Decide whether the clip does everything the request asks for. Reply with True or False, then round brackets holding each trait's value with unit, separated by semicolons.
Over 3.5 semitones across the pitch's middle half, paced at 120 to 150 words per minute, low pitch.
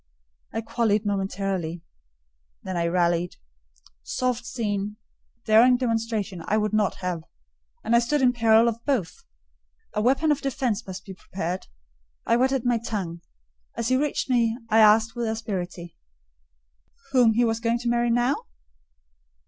False (4.6 semitones; 140 wpm; 220 Hz)